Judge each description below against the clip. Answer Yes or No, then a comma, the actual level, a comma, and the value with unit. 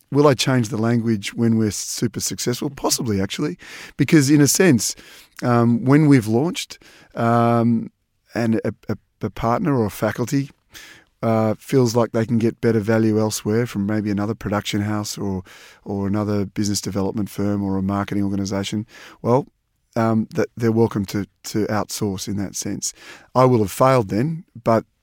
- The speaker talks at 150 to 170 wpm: Yes, average, 165 wpm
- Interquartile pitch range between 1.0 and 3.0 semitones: Yes, narrow, 2.6 semitones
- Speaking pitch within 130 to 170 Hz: No, low, 110 Hz